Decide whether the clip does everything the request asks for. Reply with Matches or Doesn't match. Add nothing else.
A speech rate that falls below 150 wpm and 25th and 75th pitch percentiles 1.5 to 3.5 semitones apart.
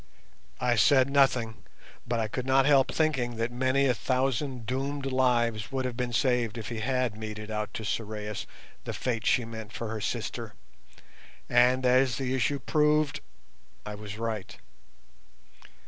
Doesn't match